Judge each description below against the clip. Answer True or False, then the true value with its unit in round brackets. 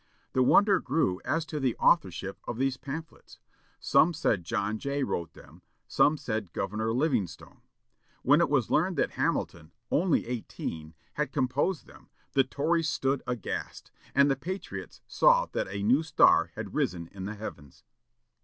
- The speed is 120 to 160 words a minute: True (155 wpm)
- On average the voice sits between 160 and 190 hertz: False (130 Hz)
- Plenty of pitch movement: True (7.3 semitones)